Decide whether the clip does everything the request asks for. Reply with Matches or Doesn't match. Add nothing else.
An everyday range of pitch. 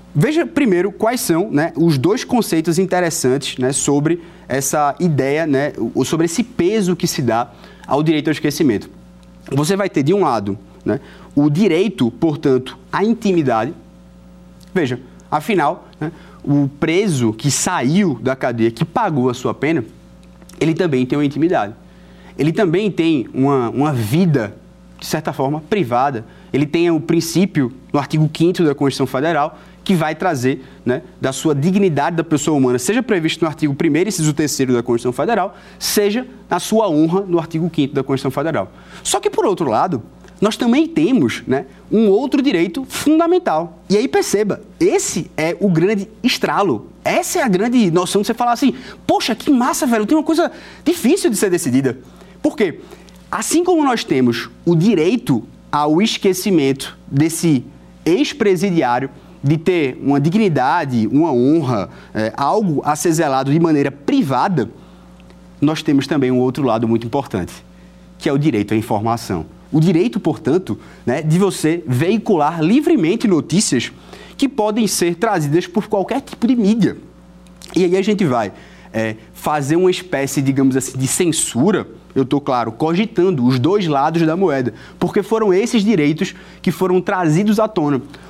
Doesn't match